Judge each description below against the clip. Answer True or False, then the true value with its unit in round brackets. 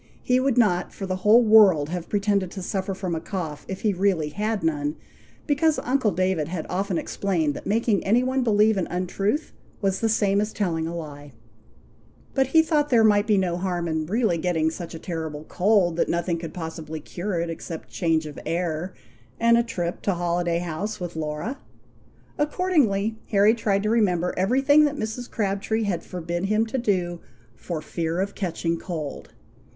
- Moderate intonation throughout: True (4.4 semitones)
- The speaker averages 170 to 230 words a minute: True (190 wpm)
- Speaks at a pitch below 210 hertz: True (190 Hz)